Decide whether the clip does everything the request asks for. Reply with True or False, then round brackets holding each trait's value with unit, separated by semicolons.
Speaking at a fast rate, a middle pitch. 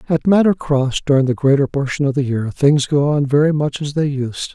True (240 wpm; 145 Hz)